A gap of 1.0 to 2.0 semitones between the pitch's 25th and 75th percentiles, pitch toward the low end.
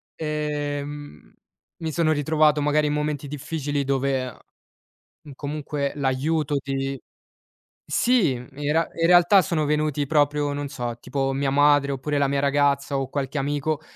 No: narrow, 1.6 semitones; medium, 145 Hz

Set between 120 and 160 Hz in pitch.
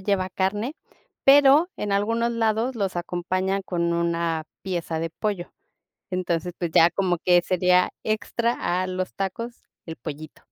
No: medium, 185 Hz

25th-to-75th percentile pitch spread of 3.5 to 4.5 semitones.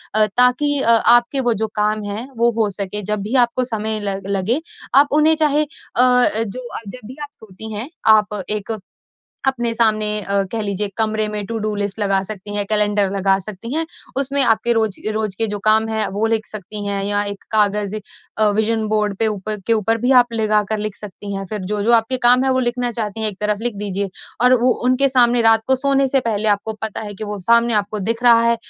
No: narrow, 2.4 semitones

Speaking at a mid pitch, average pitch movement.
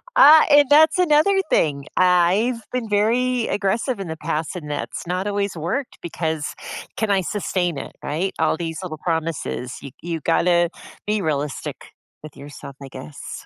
No: medium, 175 Hz; wide, 6.0 semitones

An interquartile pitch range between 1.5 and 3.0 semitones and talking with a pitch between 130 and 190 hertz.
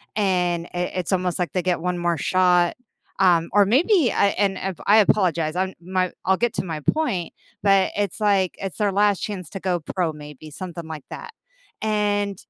Yes: average, 2.7 semitones; medium, 185 Hz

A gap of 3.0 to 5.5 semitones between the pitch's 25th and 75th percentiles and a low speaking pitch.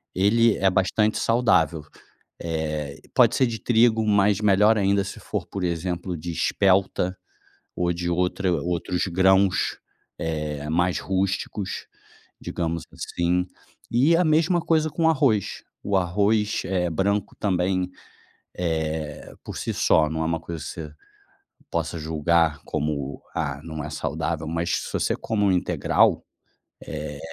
Yes: average, 4.0 semitones; very low, 90 Hz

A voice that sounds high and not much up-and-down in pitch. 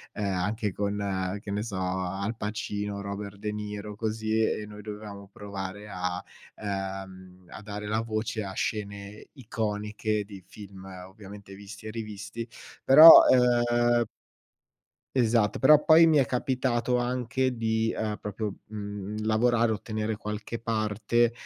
No: low, 105 Hz; narrow, 2.1 semitones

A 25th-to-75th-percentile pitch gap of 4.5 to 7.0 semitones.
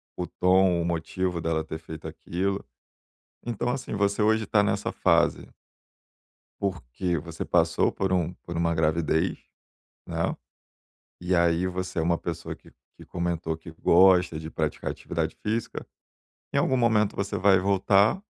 No: average, 3.0 semitones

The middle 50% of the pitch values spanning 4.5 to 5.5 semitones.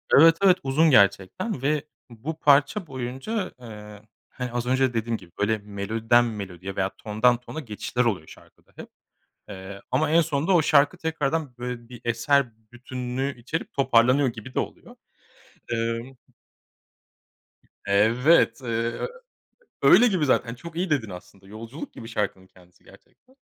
Yes: average, 4.8 semitones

